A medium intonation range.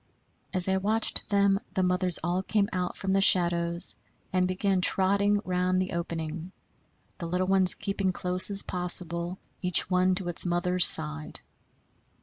No: narrow, 1.6 semitones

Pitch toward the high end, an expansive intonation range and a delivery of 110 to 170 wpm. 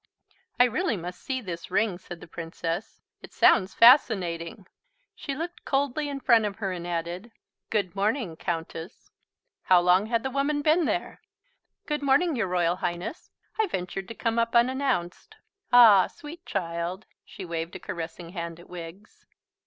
Yes: high, 195 Hz; wide, 6.9 semitones; average, 160 wpm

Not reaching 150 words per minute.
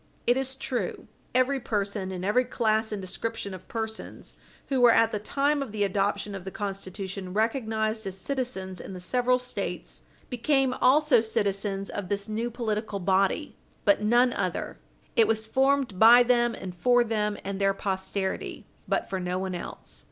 No: average, 170 wpm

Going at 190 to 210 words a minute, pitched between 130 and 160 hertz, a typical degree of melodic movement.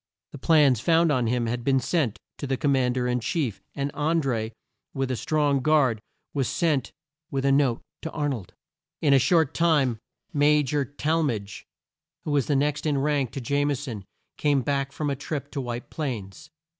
Yes: average, 195 wpm; medium, 140 Hz; average, 3.0 semitones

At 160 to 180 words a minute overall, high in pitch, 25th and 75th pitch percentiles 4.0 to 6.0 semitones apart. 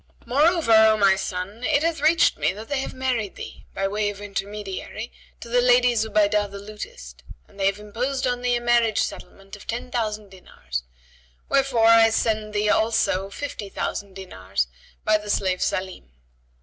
No: average, 175 wpm; high, 215 Hz; average, 3.5 semitones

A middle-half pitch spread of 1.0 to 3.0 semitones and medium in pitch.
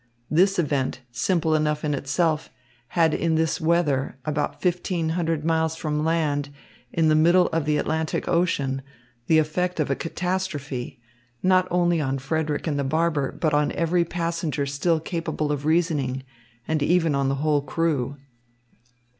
Yes: narrow, 2.5 semitones; medium, 160 Hz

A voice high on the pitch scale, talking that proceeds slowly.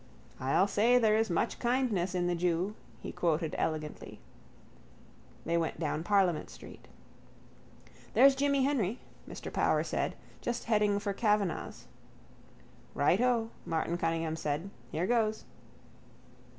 Yes: high, 195 Hz; slow, 120 wpm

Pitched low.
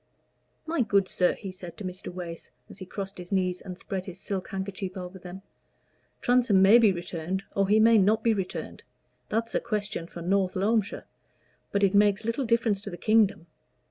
No: high, 195 Hz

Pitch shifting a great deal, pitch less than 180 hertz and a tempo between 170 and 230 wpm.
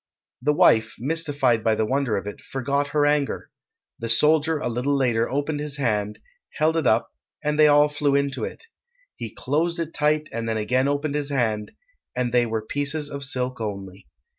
No: average, 4.4 semitones; medium, 140 Hz; average, 190 wpm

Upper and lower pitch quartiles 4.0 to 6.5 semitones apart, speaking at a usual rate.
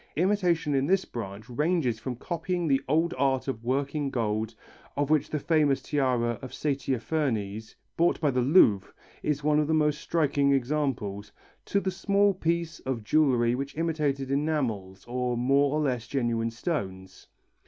Yes: average, 4.6 semitones; average, 155 wpm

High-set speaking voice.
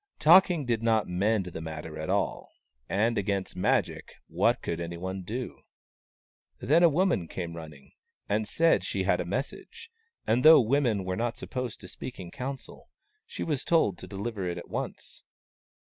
No: low, 110 Hz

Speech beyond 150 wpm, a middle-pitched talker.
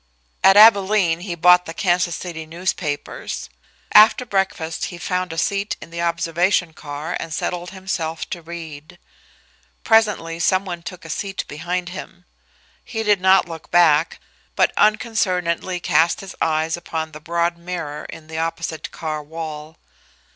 No: average, 145 wpm; medium, 170 Hz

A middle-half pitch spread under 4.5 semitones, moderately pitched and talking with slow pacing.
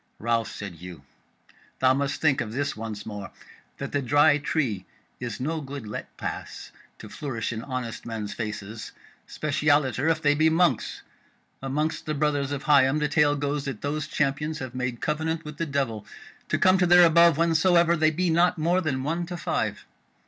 No: average, 4.1 semitones; medium, 145 Hz; average, 180 wpm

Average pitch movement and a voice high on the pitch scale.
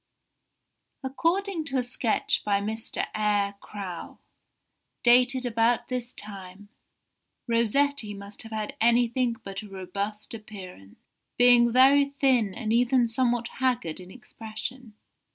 Yes: average, 3.5 semitones; high, 230 Hz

